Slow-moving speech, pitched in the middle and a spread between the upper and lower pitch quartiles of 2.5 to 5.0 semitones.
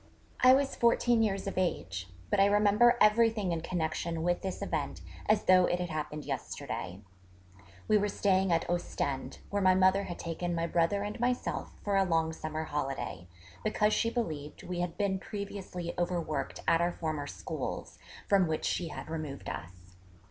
No: average, 170 wpm; medium, 175 Hz; average, 4.2 semitones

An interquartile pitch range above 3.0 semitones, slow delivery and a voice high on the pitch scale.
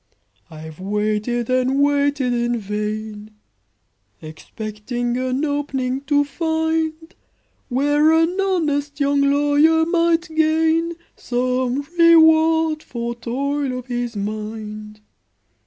Yes: average, 5.1 semitones; slow, 95 wpm; very high, 275 Hz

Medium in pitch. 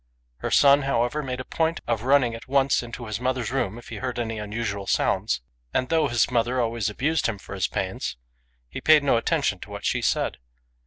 No: low, 120 Hz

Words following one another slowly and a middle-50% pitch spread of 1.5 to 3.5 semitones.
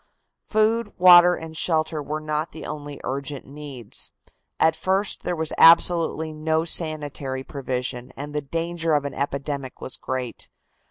No: average, 145 wpm; average, 2.9 semitones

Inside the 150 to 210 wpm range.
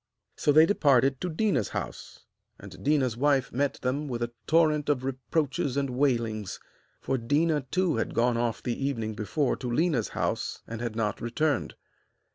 Yes: average, 165 wpm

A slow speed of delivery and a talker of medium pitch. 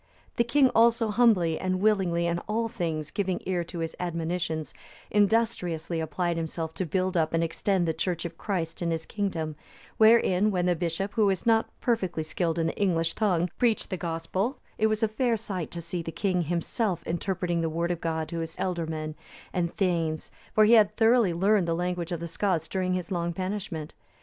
No: average, 195 wpm; medium, 180 Hz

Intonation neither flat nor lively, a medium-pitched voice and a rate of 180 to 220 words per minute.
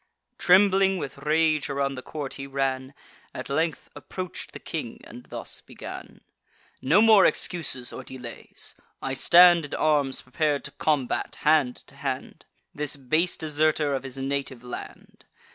No: average, 3.0 semitones; medium, 145 Hz; average, 145 wpm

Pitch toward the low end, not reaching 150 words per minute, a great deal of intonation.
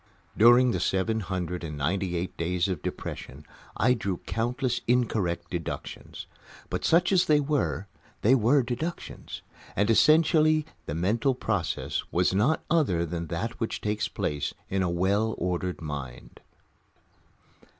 Yes: low, 100 Hz; average, 140 wpm; wide, 6.3 semitones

